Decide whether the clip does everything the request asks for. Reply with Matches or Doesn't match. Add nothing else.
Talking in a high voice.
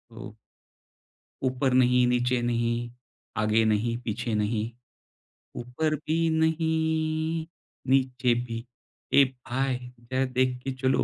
Doesn't match